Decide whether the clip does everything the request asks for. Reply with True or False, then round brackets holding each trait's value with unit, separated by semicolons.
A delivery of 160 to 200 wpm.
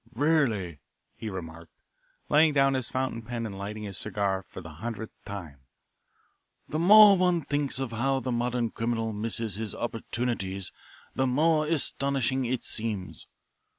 False (145 wpm)